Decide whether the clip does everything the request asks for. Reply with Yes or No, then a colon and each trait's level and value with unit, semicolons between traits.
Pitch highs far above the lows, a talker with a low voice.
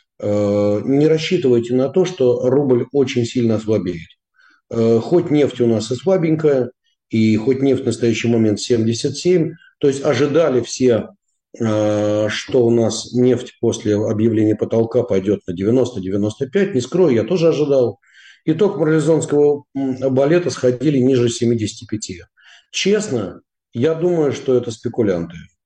No: average, 4.7 semitones; low, 125 Hz